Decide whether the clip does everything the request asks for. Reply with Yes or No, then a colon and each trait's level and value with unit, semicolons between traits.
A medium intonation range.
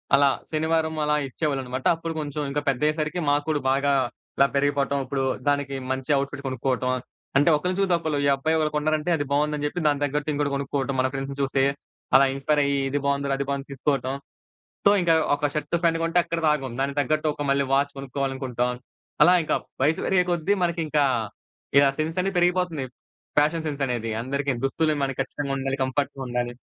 No: narrow, 2.2 semitones